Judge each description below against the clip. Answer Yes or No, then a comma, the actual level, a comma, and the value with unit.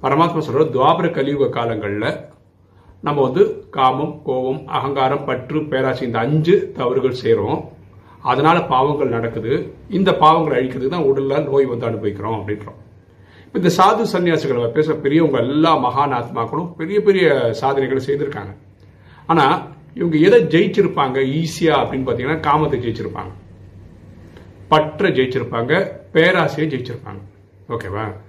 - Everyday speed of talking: Yes, average, 110 wpm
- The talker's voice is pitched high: No, low, 135 Hz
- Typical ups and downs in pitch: No, wide, 6.4 semitones